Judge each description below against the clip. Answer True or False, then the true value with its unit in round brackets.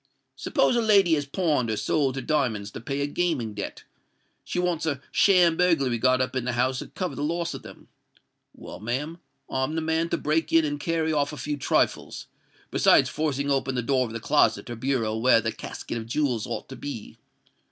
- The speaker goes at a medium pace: False (210 wpm)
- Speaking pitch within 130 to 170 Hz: True (140 Hz)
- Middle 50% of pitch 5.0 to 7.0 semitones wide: False (4.6 semitones)